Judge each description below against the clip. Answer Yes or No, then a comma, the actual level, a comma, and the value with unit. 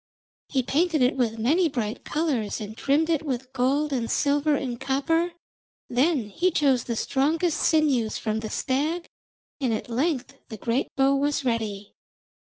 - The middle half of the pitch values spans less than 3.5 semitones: No, average, 4.4 semitones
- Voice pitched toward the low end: No, very high, 270 Hz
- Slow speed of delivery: No, average, 160 wpm